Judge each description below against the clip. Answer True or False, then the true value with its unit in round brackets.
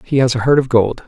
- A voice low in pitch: True (125 Hz)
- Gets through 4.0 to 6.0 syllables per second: False (6.2 syllables/s)